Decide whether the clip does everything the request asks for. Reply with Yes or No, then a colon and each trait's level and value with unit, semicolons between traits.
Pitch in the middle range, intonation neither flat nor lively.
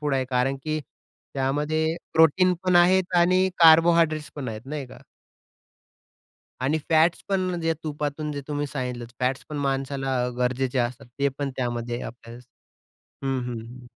Yes: medium, 145 Hz; average, 3.9 semitones